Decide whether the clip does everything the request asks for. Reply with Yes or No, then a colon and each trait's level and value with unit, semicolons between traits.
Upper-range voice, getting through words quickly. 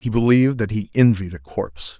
No: low, 105 Hz; fast, 210 wpm